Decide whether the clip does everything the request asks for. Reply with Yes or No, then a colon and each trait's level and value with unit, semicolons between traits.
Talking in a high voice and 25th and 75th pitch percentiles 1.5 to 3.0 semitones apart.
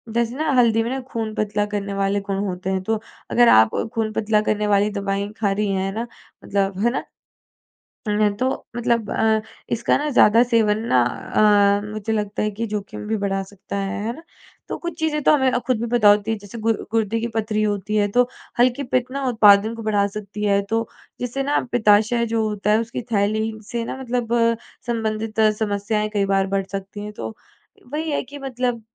Yes: high, 215 Hz; narrow, 2.4 semitones